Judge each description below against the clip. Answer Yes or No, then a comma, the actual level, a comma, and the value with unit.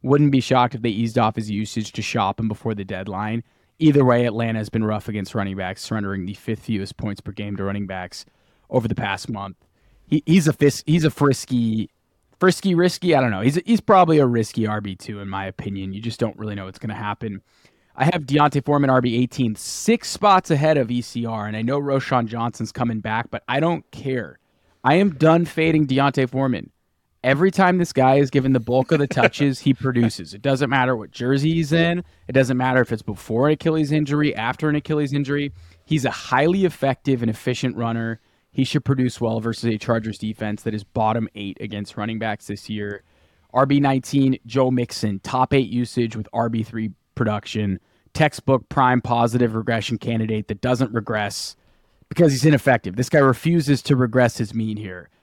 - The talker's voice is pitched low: Yes, low, 120 Hz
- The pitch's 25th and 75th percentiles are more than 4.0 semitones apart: Yes, average, 4.6 semitones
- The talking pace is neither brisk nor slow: Yes, average, 195 wpm